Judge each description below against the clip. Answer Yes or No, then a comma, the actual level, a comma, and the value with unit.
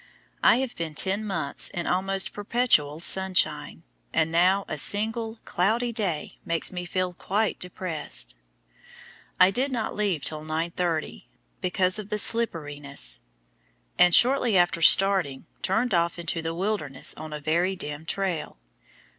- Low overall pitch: No, medium, 180 Hz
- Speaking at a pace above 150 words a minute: No, average, 140 wpm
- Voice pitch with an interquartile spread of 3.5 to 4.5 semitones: Yes, average, 4.2 semitones